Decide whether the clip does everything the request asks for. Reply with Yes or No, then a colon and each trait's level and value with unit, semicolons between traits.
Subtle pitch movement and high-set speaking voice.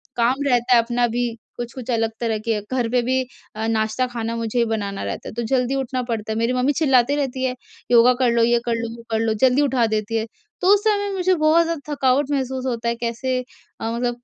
Yes: narrow, 2.2 semitones; high, 245 Hz